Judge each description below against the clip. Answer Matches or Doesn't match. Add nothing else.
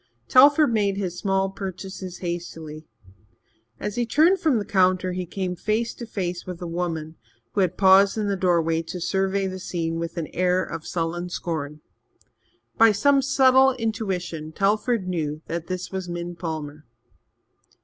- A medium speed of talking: Matches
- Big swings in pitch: Doesn't match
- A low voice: Doesn't match